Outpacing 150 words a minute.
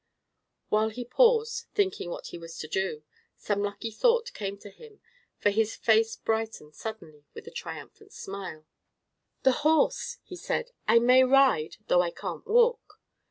Yes: average, 160 wpm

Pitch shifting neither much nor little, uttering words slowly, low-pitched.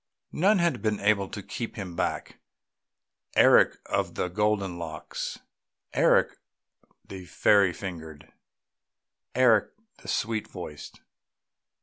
Yes: average, 3.4 semitones; slow, 105 wpm; low, 100 Hz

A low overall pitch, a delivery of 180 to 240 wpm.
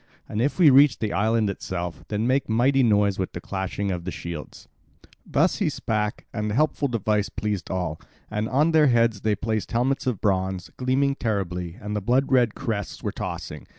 Yes: low, 110 Hz; average, 185 wpm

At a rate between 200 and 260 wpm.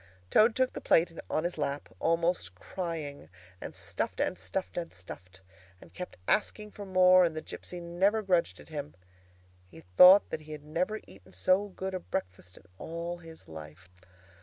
No: average, 175 wpm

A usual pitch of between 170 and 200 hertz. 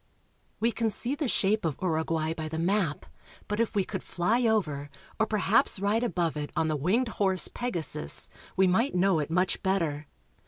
Yes: high, 190 Hz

